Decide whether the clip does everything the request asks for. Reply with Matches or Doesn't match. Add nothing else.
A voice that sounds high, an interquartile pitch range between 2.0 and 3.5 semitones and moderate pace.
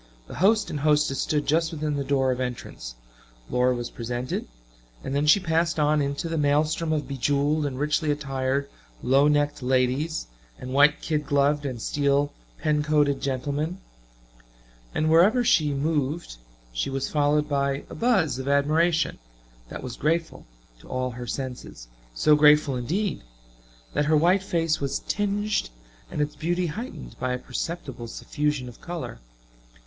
Doesn't match